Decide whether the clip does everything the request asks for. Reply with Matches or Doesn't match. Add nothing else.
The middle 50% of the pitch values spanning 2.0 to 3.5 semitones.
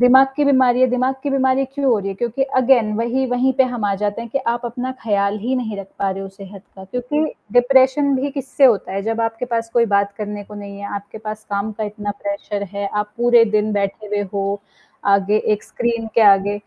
Doesn't match